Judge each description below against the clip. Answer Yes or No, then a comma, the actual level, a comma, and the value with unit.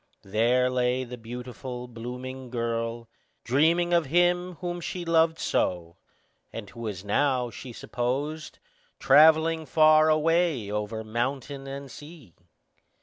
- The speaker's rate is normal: No, slow, 120 wpm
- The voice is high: No, low, 130 Hz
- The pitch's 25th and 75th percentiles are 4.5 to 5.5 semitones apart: Yes, average, 5.2 semitones